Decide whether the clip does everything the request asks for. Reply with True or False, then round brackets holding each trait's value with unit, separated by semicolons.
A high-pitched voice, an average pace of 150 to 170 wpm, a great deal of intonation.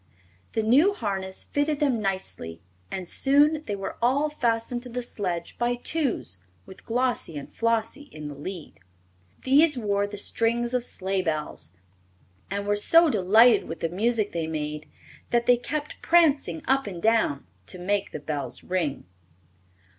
True (220 Hz; 155 wpm; 5.8 semitones)